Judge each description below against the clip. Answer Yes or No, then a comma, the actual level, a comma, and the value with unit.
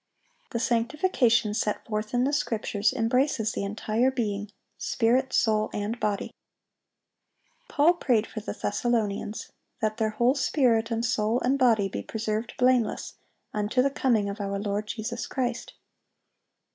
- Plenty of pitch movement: No, average, 2.9 semitones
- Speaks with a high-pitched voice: Yes, high, 225 Hz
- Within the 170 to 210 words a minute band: No, slow, 135 wpm